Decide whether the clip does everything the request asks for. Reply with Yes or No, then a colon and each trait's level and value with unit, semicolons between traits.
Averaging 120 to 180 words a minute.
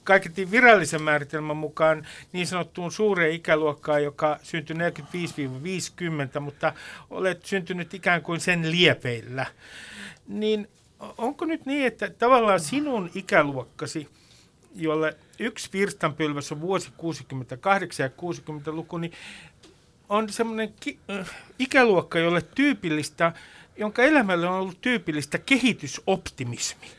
No: average, 105 wpm